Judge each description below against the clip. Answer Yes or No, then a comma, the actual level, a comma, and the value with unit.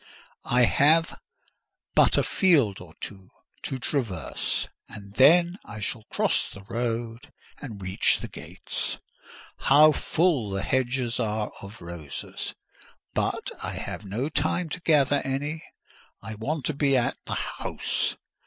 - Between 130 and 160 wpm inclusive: Yes, slow, 135 wpm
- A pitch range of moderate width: No, wide, 5.9 semitones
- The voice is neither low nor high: No, low, 120 Hz